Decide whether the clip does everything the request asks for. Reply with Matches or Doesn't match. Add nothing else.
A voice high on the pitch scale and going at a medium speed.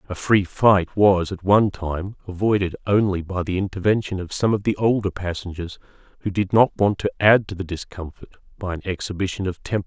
Doesn't match